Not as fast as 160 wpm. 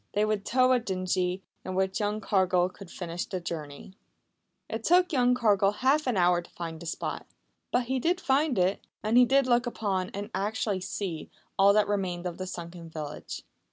No: average, 190 wpm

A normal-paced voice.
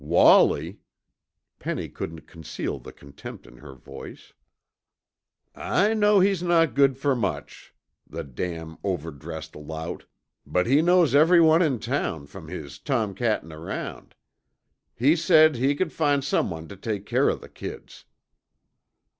No: slow, 130 wpm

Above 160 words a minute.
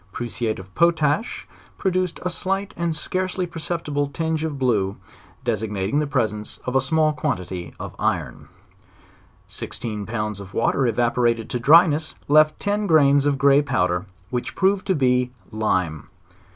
No: average, 155 wpm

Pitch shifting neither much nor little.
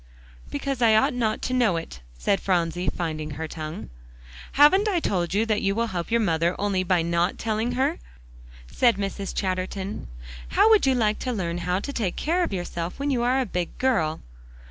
No: wide, 6.1 semitones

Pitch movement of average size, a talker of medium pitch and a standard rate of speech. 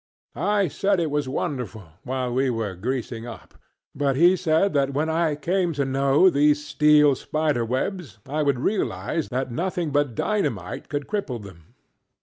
Yes: average, 4.1 semitones; medium, 145 Hz; average, 160 wpm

